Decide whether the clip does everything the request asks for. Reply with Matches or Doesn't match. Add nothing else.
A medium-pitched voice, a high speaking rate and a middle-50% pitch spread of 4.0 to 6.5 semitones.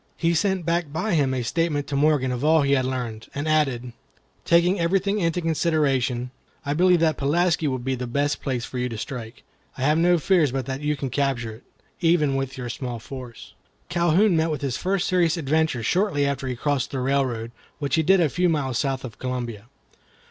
Matches